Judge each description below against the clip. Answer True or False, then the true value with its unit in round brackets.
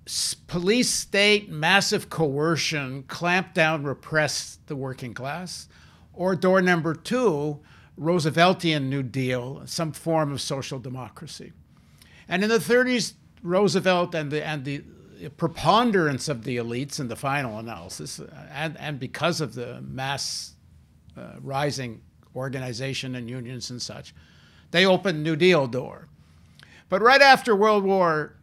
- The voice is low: False (150 Hz)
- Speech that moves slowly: True (130 wpm)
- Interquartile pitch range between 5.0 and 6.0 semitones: True (5.4 semitones)